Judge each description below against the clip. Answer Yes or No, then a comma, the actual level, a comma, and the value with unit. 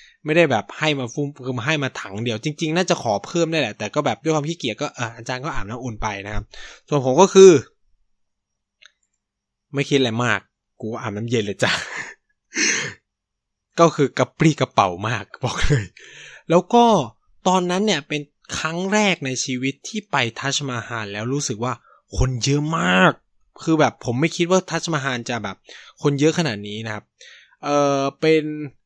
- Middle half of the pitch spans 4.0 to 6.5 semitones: Yes, average, 4.9 semitones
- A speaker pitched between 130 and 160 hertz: Yes, medium, 140 Hz